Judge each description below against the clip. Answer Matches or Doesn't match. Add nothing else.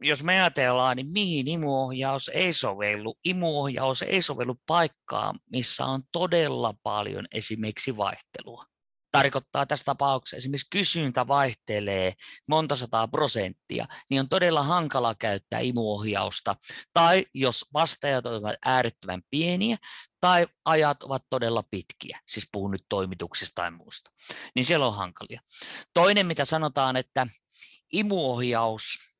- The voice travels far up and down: Matches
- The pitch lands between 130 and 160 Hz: Matches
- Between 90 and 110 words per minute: Doesn't match